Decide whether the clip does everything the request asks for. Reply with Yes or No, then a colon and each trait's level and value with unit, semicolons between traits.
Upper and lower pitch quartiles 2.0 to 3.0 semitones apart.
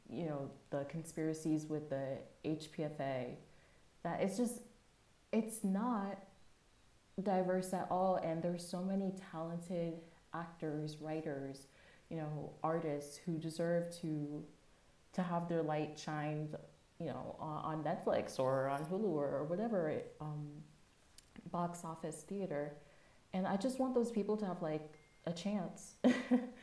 No: average, 3.8 semitones